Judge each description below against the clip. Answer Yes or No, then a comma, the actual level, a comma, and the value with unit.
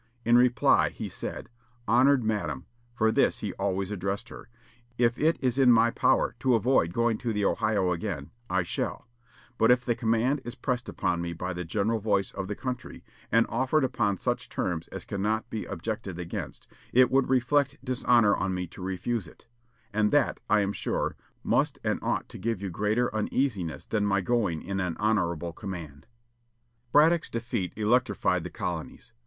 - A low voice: Yes, low, 110 Hz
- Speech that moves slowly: No, average, 175 wpm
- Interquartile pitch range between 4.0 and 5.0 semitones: Yes, average, 4.6 semitones